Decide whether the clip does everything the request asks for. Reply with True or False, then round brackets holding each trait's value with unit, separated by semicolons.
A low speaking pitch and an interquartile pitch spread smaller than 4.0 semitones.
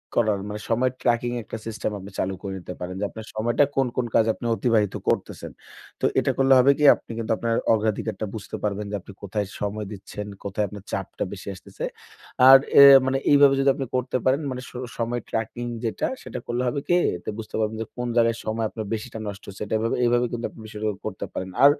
True (110 Hz; 2.7 semitones)